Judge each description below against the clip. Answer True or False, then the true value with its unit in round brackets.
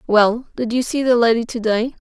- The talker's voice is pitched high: True (235 Hz)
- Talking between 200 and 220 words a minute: False (230 wpm)